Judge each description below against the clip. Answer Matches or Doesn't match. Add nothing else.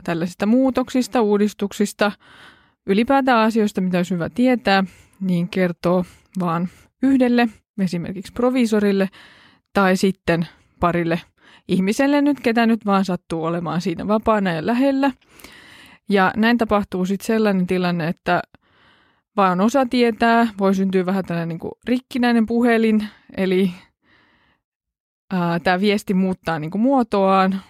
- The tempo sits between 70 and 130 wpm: Matches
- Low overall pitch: Doesn't match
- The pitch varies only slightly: Doesn't match